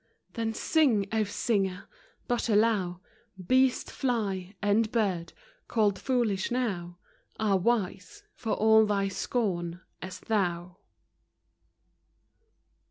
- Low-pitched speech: No, high, 205 Hz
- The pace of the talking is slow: Yes, slow, 100 wpm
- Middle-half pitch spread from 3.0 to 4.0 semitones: Yes, average, 3.7 semitones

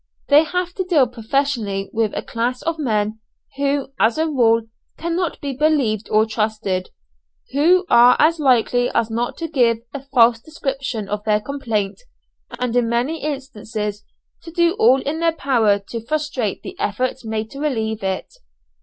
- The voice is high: Yes, high, 245 Hz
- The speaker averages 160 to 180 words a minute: Yes, average, 165 wpm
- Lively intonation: No, average, 5.0 semitones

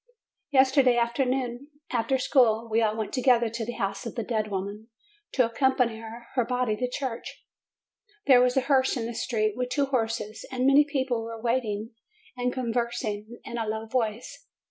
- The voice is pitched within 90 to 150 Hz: No, high, 240 Hz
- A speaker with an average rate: Yes, average, 175 wpm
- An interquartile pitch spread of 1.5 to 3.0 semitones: Yes, narrow, 2.4 semitones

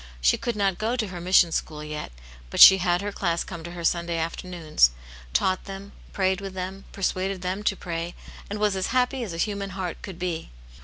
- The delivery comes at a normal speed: No, fast, 215 wpm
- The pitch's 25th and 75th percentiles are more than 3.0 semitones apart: No, narrow, 2.5 semitones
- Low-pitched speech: No, medium, 185 Hz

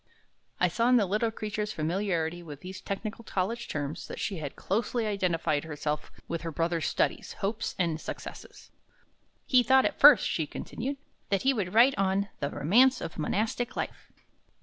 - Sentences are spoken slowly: No, average, 170 wpm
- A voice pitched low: No, high, 195 Hz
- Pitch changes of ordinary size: No, wide, 5.7 semitones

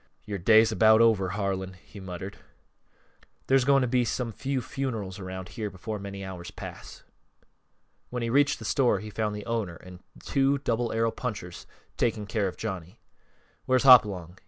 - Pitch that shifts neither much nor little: Yes, average, 4.2 semitones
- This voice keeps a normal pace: Yes, average, 165 wpm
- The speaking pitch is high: No, low, 105 Hz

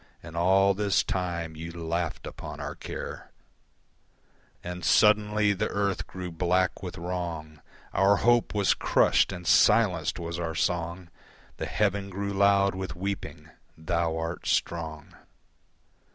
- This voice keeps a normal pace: No, slow, 130 wpm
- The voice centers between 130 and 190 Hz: No, very low, 90 Hz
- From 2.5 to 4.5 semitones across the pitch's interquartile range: Yes, average, 2.8 semitones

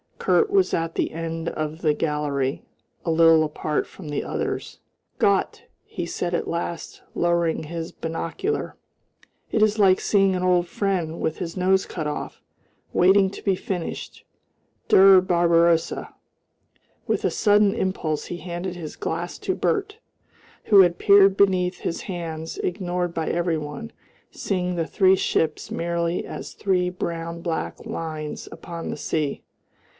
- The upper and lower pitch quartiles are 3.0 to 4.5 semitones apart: No, narrow, 2.5 semitones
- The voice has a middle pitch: Yes, medium, 170 Hz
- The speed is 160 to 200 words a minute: No, average, 145 wpm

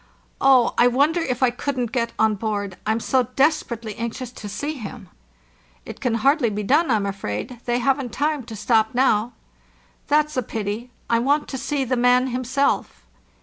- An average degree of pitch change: Yes, average, 3.6 semitones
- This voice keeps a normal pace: Yes, average, 175 wpm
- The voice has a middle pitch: No, high, 245 Hz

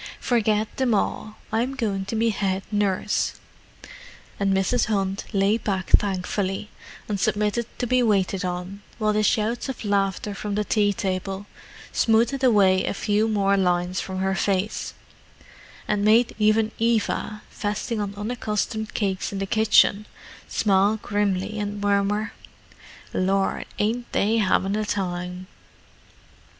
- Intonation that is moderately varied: No, narrow, 1.9 semitones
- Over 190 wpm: No, slow, 135 wpm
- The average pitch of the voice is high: Yes, high, 205 Hz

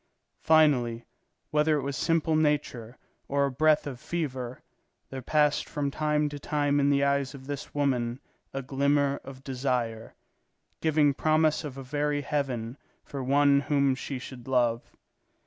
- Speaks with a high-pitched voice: No, medium, 140 Hz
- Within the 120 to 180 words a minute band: Yes, average, 150 wpm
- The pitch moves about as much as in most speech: No, narrow, 2.2 semitones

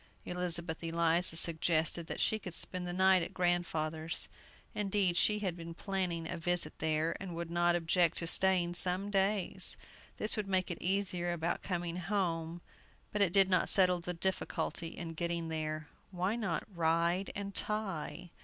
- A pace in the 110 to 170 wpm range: Yes, average, 165 wpm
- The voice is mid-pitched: Yes, medium, 175 Hz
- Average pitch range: No, narrow, 2.3 semitones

